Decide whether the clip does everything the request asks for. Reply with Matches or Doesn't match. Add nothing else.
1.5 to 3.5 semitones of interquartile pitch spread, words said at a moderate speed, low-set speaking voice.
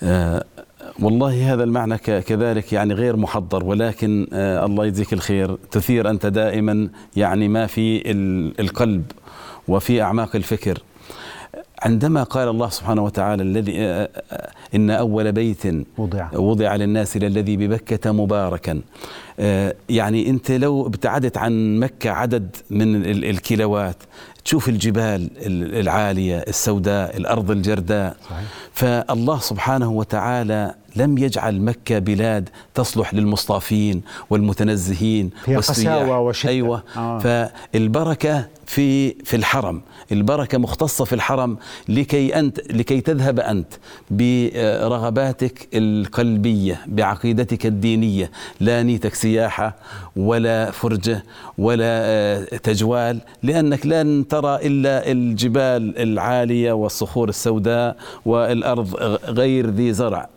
Matches